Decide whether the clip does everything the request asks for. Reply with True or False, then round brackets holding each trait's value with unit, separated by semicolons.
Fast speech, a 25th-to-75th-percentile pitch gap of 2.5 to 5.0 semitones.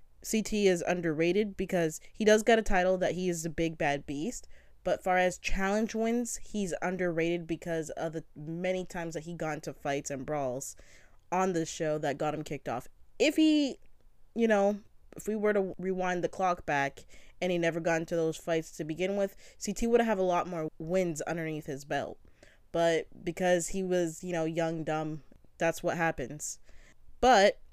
False (190 wpm; 2.9 semitones)